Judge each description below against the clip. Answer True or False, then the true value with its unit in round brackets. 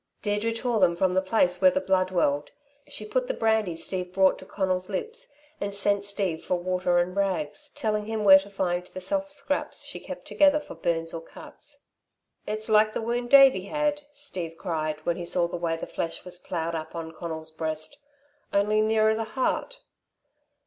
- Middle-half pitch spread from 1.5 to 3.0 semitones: False (4.2 semitones)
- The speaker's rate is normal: True (190 wpm)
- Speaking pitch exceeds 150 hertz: True (190 Hz)